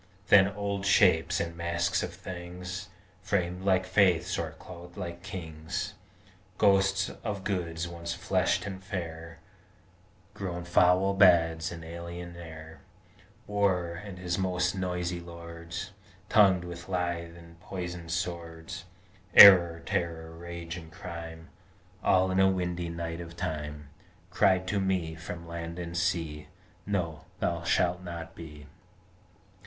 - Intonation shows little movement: Yes, narrow, 1.8 semitones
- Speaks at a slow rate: Yes, slow, 125 wpm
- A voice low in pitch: Yes, very low, 85 Hz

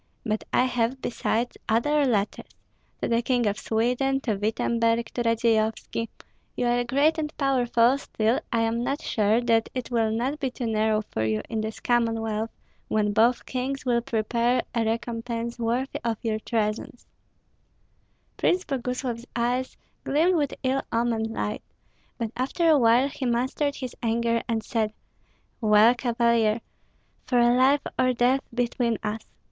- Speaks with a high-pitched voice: Yes, high, 235 Hz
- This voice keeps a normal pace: Yes, average, 150 wpm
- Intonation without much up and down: Yes, narrow, 2.2 semitones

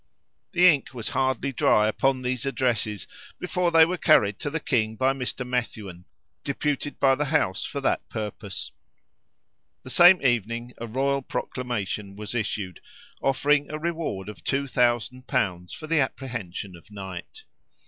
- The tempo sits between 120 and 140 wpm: No, average, 150 wpm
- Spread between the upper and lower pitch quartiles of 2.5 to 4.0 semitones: No, average, 4.8 semitones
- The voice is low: Yes, low, 125 Hz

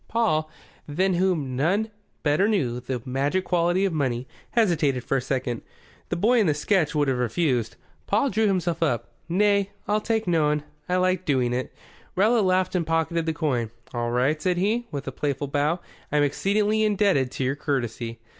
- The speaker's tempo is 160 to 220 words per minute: Yes, average, 180 wpm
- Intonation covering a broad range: Yes, wide, 6.2 semitones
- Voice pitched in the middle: Yes, medium, 160 Hz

